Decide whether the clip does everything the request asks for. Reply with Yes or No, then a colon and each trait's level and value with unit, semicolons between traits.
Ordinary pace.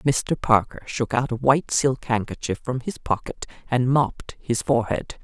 Yes: average, 170 wpm